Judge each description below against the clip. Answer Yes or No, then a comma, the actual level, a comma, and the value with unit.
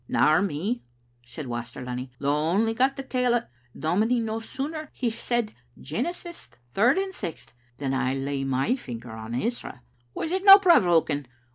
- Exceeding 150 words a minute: Yes, average, 170 wpm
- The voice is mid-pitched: No, high, 195 Hz